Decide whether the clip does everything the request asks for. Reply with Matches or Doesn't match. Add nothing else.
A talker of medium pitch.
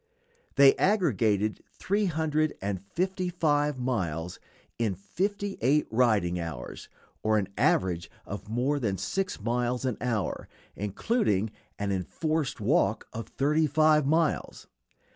Doesn't match